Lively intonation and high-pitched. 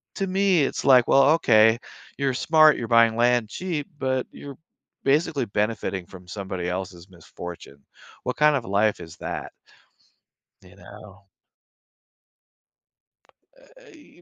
No: wide, 6.7 semitones; low, 120 Hz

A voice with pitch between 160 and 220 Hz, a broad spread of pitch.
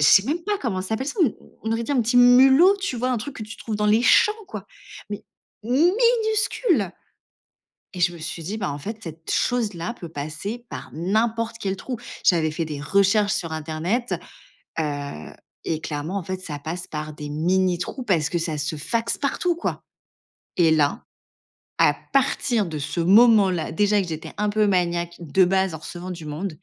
Yes: high, 190 Hz; wide, 6.3 semitones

